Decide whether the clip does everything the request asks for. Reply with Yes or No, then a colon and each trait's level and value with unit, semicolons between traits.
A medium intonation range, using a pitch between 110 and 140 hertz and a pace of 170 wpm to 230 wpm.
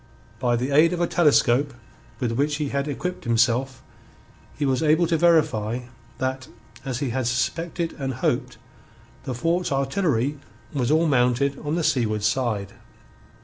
No: average, 4.2 semitones; low, 135 Hz; average, 150 wpm